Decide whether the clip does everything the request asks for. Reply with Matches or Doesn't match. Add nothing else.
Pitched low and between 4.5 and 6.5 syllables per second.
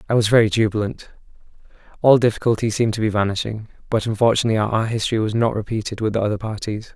Doesn't match